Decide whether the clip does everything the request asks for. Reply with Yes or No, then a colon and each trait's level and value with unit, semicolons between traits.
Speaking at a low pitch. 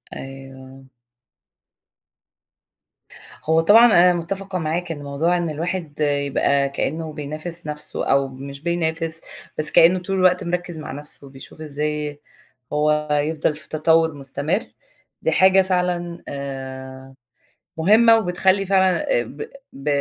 No: medium, 155 Hz